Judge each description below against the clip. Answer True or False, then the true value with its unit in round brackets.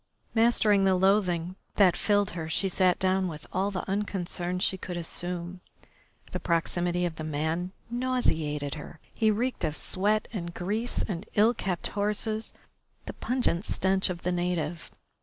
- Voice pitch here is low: False (185 Hz)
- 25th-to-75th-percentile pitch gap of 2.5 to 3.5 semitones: True (3.1 semitones)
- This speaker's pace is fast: False (155 wpm)